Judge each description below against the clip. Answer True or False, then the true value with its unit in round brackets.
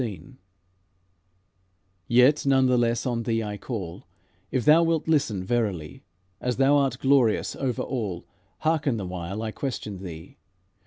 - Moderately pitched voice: False (120 Hz)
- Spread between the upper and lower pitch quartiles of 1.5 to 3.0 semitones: False (5.1 semitones)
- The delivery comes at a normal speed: True (145 wpm)